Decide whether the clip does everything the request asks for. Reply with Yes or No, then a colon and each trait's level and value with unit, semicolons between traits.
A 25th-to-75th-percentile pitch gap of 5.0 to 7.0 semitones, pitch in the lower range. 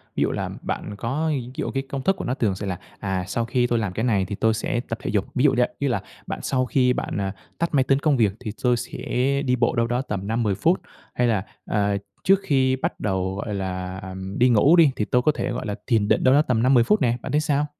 No: average, 4.4 semitones; low, 120 Hz